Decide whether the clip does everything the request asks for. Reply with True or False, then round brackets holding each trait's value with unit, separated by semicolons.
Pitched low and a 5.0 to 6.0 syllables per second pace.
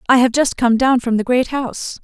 False (250 Hz; 5.5 syllables/s)